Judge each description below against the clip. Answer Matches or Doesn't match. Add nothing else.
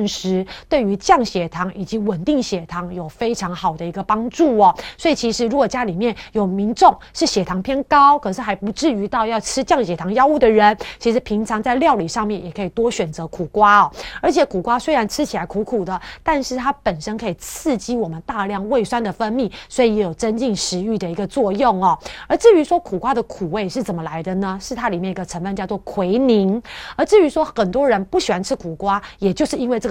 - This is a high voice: Matches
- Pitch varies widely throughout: Doesn't match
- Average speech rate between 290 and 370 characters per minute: Matches